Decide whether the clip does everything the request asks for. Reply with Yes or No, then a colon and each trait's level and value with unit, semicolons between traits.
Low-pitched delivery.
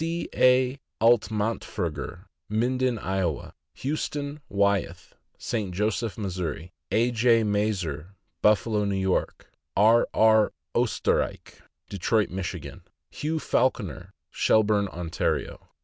Yes: low, 105 Hz